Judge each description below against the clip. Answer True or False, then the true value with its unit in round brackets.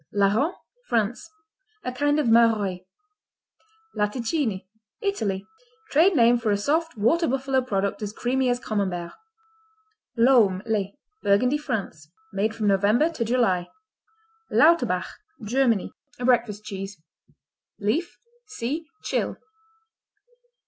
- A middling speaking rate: False (105 wpm)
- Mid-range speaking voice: False (230 Hz)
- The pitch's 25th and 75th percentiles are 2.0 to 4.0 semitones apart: False (4.8 semitones)